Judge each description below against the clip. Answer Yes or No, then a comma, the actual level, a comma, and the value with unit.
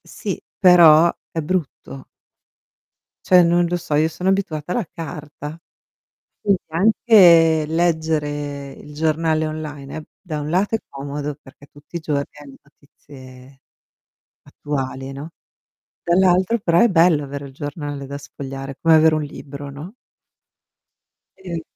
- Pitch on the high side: No, medium, 155 Hz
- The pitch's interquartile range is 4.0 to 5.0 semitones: No, average, 3.1 semitones